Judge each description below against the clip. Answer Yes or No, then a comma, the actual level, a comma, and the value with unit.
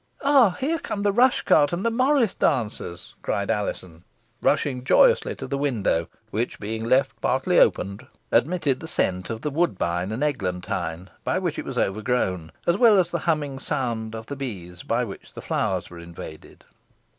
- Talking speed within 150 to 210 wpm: Yes, average, 175 wpm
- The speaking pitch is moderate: No, low, 125 Hz